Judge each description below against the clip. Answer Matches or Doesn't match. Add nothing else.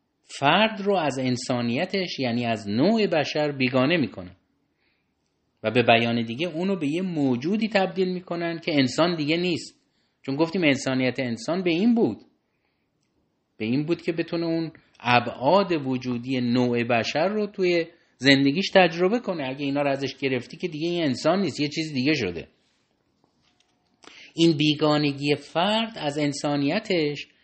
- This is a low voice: Doesn't match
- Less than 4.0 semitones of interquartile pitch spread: Doesn't match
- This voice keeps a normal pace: Matches